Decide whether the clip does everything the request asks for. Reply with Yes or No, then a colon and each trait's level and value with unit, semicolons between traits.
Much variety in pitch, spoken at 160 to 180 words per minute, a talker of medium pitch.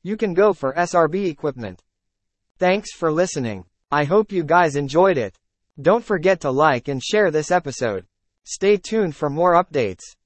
Yes: wide, 6.0 semitones; average, 165 wpm; medium, 165 Hz